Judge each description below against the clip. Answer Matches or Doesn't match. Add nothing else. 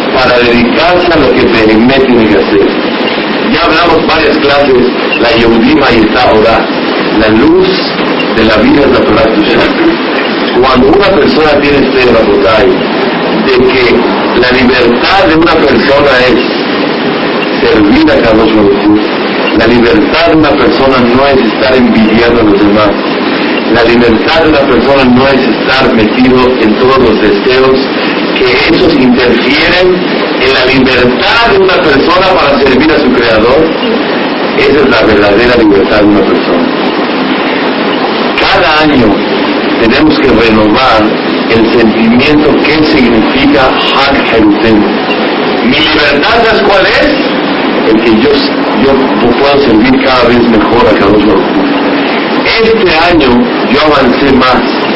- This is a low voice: Matches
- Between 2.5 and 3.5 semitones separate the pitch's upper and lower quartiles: Matches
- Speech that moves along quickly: Doesn't match